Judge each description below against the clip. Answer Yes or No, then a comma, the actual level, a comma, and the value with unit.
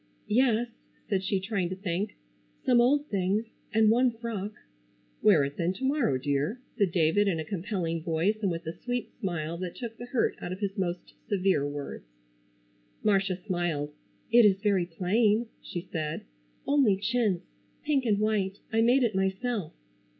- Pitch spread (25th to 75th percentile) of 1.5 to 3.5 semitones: No, average, 4.5 semitones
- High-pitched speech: Yes, high, 195 Hz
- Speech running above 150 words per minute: Yes, average, 165 wpm